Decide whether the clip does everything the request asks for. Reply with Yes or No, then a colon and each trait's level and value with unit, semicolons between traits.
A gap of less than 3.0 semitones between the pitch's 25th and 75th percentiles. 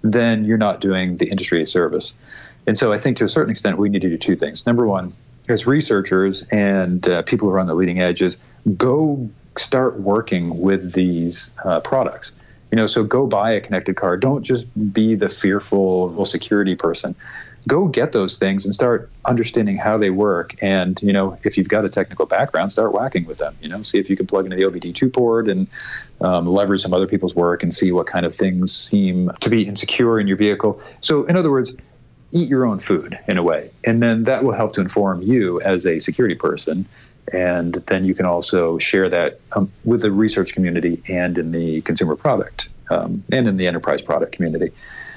No: average, 3.9 semitones